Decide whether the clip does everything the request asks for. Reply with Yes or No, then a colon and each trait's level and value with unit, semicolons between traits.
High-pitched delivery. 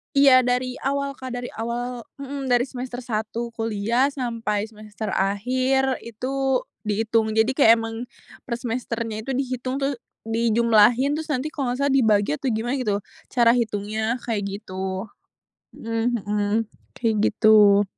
Yes: high, 235 Hz